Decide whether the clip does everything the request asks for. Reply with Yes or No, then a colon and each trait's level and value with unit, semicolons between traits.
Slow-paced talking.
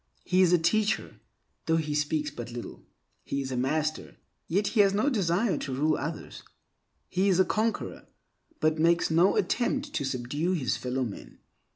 No: average, 175 wpm